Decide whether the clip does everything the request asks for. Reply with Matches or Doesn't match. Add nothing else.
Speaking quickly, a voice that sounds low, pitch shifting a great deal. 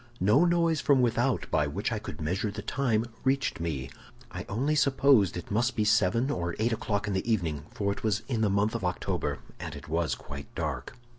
Matches